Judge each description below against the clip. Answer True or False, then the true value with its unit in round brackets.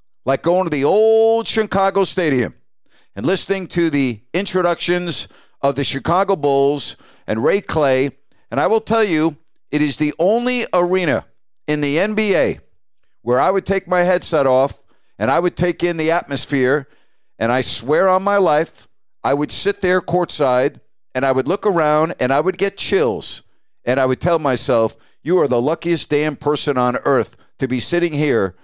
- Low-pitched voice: False (160 Hz)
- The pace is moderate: True (175 wpm)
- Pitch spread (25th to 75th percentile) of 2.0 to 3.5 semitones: False (5.2 semitones)